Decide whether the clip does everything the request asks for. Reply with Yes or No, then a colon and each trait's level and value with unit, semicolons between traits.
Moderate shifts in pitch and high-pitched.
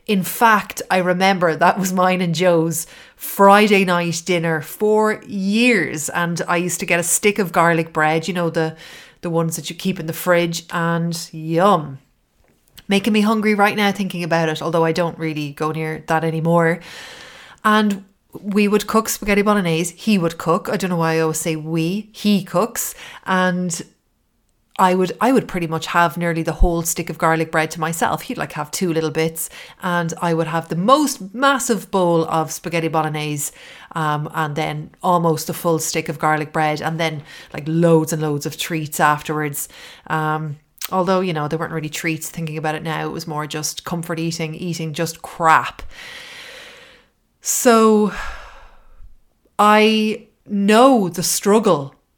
No: average, 3.7 semitones; medium, 170 Hz